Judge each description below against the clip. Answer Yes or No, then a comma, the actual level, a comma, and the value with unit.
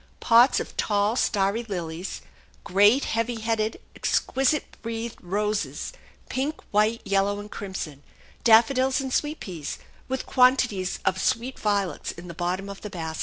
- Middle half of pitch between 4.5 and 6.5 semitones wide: No, average, 3.9 semitones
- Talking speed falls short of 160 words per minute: Yes, average, 140 wpm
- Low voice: No, high, 210 Hz